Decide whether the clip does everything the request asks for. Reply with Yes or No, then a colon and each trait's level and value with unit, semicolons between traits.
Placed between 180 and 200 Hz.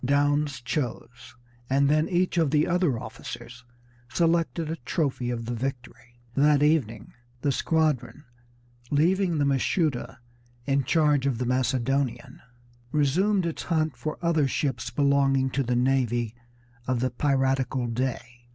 No: medium, 140 Hz